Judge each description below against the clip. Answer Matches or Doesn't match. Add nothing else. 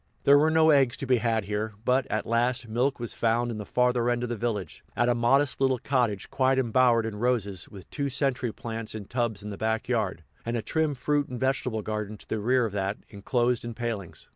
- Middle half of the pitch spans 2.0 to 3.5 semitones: Matches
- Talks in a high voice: Doesn't match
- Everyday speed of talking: Doesn't match